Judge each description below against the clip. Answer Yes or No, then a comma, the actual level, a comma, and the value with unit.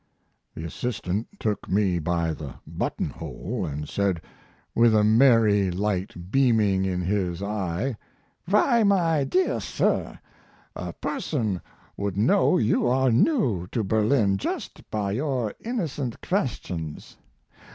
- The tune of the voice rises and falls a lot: Yes, wide, 5.9 semitones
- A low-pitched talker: Yes, low, 105 Hz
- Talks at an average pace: No, slow, 120 wpm